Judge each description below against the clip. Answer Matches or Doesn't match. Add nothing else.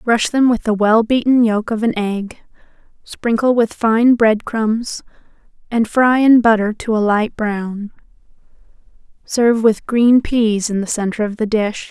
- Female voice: Matches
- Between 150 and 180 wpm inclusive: Matches